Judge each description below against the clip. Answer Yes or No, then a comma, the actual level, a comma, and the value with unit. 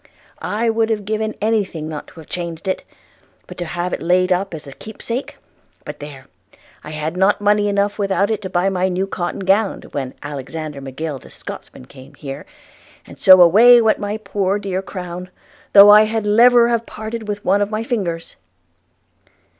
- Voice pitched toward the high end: Yes, high, 195 Hz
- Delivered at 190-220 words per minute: Yes, average, 195 wpm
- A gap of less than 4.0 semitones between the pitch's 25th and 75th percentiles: No, average, 4.3 semitones